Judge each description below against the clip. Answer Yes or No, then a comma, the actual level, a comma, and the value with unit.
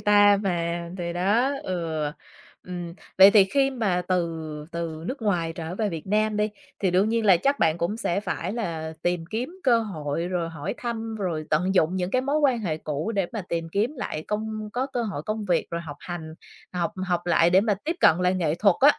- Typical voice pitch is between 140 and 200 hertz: Yes, medium, 185 Hz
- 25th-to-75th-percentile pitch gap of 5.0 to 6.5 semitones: No, average, 4.4 semitones